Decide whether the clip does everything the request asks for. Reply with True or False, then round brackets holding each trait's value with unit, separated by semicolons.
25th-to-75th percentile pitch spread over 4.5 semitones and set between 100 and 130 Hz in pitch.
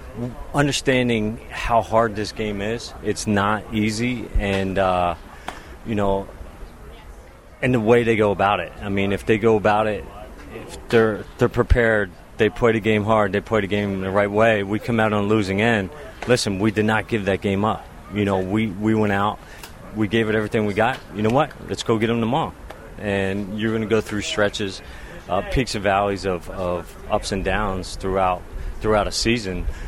False (2.5 semitones; 105 Hz)